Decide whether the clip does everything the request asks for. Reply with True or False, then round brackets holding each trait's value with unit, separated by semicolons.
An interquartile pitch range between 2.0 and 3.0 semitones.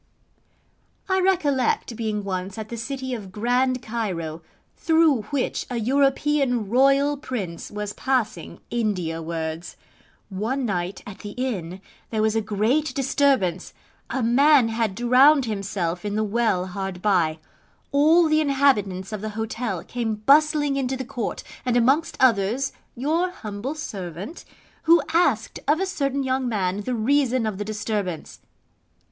False (5.3 semitones)